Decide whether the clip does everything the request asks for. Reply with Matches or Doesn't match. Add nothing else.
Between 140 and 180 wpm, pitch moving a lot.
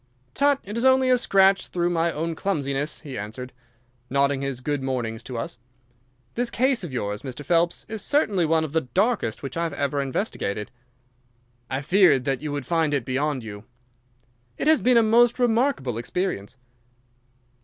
Matches